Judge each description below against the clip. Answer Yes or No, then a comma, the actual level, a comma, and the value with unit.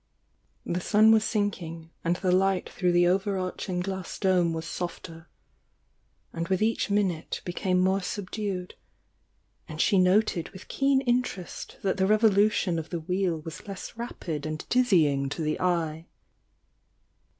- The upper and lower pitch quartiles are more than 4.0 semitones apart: No, average, 3.3 semitones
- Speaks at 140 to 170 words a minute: Yes, average, 150 wpm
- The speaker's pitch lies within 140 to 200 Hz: Yes, medium, 185 Hz